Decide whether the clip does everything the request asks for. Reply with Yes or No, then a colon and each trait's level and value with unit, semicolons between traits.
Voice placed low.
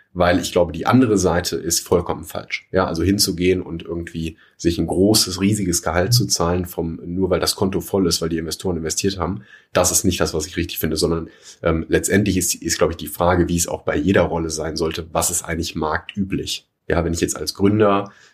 Yes: very low, 85 Hz